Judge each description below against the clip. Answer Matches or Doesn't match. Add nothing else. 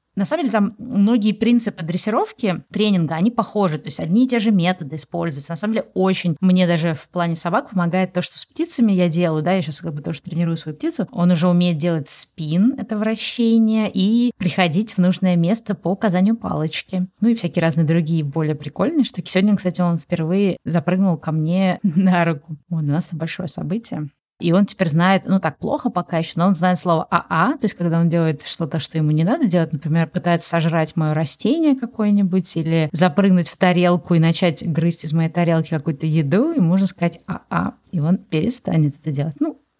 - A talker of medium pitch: Matches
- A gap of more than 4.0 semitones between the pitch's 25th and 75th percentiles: Doesn't match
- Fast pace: Matches